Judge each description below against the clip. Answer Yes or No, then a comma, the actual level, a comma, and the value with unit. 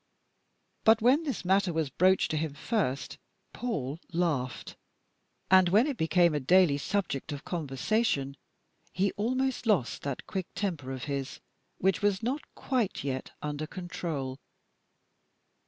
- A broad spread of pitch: Yes, wide, 6.5 semitones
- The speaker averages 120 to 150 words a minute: Yes, average, 140 wpm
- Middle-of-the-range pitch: Yes, medium, 175 Hz